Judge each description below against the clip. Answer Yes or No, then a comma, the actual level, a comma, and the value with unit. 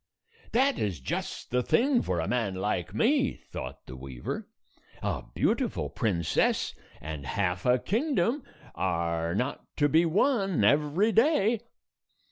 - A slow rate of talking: Yes, slow, 130 wpm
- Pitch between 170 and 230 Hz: No, low, 125 Hz